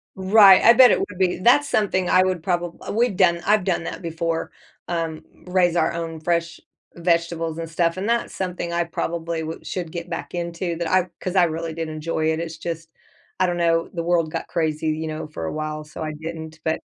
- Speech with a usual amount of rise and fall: No, narrow, 2.1 semitones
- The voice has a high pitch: No, medium, 170 Hz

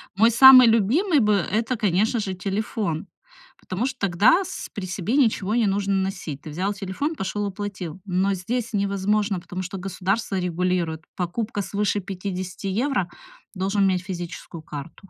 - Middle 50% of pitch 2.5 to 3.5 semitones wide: Yes, average, 2.9 semitones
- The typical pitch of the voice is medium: No, high, 195 Hz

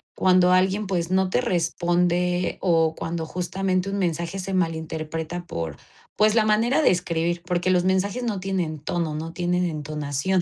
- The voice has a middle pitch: Yes, medium, 180 Hz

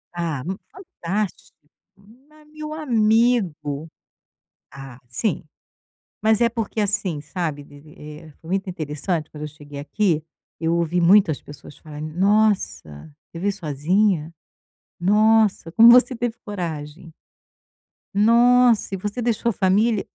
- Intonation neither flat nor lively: No, wide, 6.2 semitones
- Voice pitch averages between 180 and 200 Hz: Yes, medium, 185 Hz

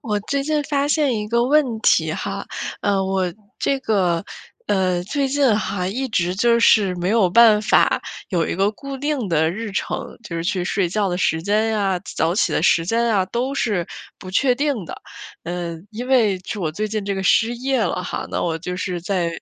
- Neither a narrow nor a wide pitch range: Yes, average, 4.7 semitones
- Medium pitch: No, high, 205 Hz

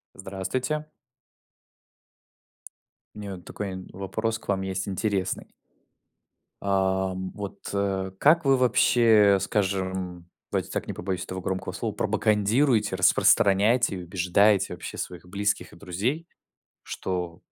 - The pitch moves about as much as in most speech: No, narrow, 2.3 semitones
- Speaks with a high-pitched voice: No, low, 100 Hz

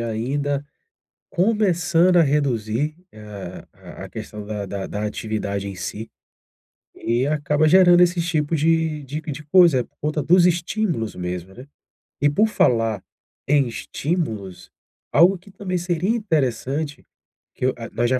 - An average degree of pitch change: No, wide, 7.0 semitones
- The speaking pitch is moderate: Yes, medium, 145 Hz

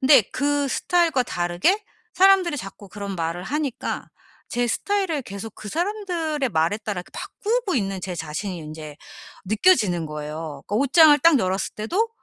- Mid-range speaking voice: No, high, 225 Hz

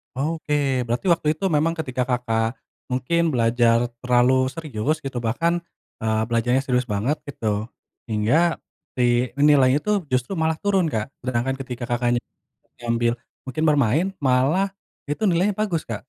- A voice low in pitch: Yes, low, 130 Hz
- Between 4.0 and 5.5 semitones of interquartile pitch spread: Yes, average, 4.7 semitones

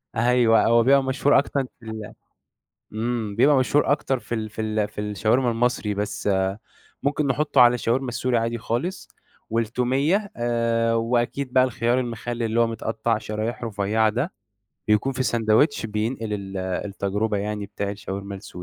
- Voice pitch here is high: No, low, 115 Hz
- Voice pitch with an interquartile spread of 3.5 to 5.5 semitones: No, average, 2.8 semitones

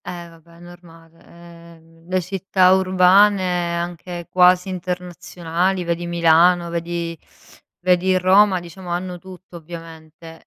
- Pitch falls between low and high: Yes, medium, 175 Hz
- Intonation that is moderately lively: No, narrow, 1.4 semitones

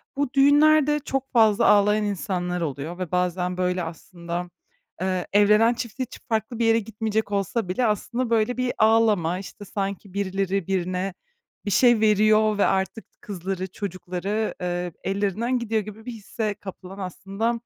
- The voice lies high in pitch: Yes, high, 205 Hz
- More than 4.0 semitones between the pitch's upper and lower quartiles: No, average, 3.5 semitones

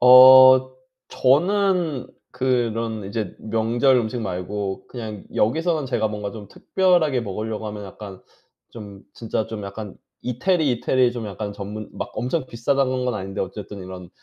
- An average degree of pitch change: Yes, average, 3.9 semitones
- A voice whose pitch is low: Yes, low, 115 Hz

